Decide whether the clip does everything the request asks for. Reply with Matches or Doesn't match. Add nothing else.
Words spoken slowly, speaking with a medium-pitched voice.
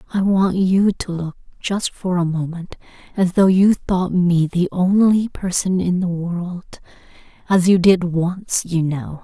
Doesn't match